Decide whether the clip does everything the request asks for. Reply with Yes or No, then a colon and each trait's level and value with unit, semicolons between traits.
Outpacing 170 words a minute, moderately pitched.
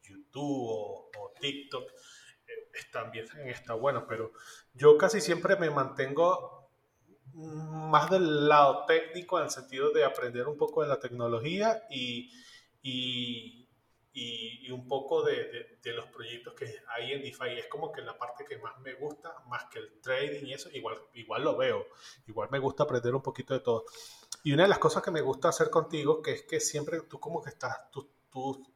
Yes: fast, 190 wpm; medium, 155 Hz